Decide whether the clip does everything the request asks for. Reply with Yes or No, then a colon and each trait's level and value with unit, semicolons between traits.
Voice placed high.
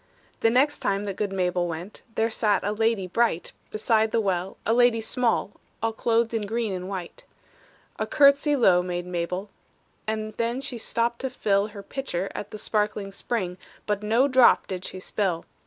Yes: high, 215 Hz